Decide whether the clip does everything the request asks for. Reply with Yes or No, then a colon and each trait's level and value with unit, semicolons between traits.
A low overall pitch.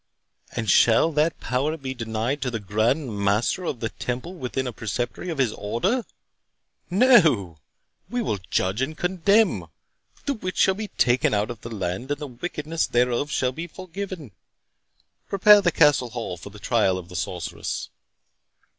Yes: low, 130 Hz